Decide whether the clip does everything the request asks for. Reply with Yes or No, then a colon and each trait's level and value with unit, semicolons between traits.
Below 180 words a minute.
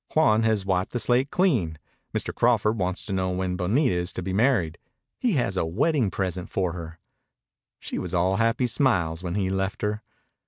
No: average, 190 wpm